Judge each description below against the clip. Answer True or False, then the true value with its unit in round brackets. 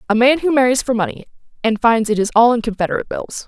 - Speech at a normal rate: False (240 wpm)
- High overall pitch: True (235 Hz)